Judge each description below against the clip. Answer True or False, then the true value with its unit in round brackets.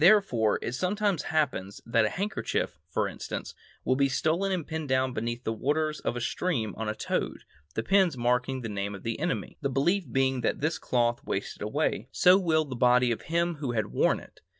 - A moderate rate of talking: False (210 wpm)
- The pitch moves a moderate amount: False (5.7 semitones)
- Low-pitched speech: True (130 Hz)